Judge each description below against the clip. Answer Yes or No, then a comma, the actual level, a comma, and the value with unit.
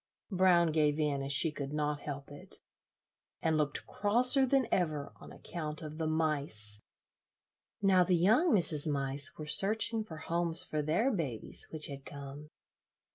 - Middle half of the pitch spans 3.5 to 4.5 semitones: Yes, average, 3.8 semitones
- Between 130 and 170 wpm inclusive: Yes, average, 155 wpm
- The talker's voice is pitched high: No, medium, 155 Hz